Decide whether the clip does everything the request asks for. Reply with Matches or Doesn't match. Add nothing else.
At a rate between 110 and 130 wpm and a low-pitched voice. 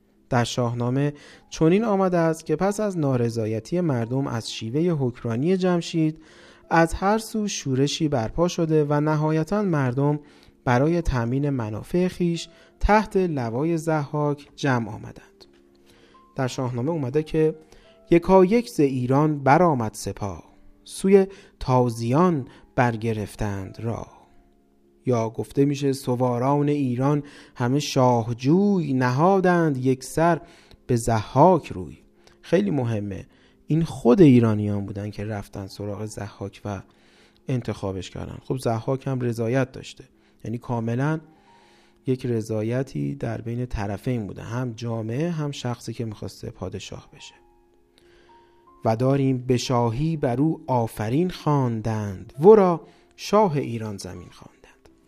Matches